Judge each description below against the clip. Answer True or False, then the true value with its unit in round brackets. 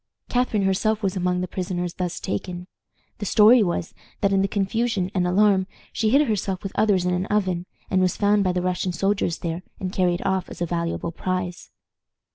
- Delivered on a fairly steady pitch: True (2.3 semitones)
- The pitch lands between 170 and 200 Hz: True (185 Hz)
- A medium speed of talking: True (195 wpm)